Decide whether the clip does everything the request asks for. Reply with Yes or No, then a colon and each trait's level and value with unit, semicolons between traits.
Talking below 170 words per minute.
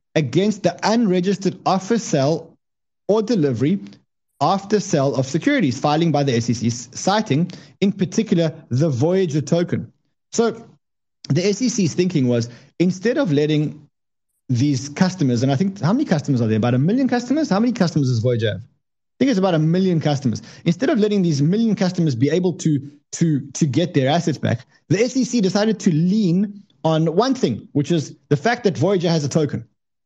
No: average, 175 wpm